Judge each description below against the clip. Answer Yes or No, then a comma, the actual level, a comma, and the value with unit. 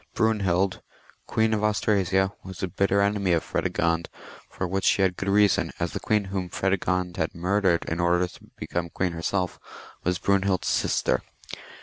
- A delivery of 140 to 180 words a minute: Yes, average, 165 wpm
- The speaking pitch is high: No, very low, 95 Hz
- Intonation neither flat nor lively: No, narrow, 2.1 semitones